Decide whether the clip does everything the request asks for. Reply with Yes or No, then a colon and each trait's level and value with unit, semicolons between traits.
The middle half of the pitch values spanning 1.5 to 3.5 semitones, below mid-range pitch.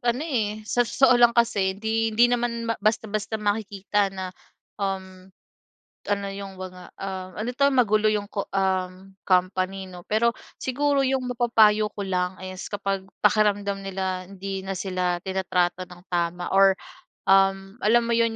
No: average, 2.9 semitones; high, 200 Hz